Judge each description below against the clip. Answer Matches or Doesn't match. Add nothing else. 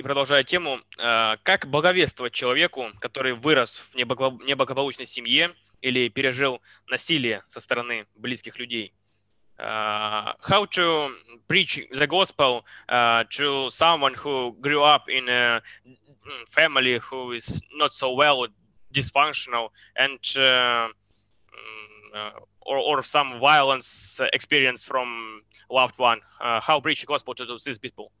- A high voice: Doesn't match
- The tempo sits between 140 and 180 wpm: Doesn't match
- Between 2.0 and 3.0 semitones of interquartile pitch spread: Doesn't match